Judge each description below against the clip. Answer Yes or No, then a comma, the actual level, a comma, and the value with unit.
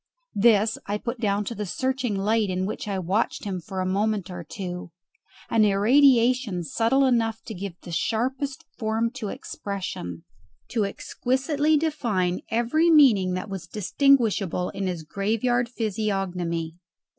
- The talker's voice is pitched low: No, high, 210 Hz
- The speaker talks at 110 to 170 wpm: Yes, average, 145 wpm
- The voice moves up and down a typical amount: Yes, average, 4.4 semitones